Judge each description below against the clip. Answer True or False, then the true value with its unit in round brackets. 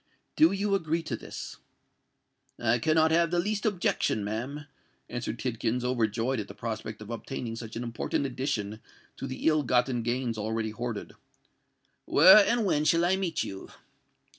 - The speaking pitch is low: True (125 Hz)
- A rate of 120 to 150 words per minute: False (160 wpm)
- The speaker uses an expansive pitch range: True (6.2 semitones)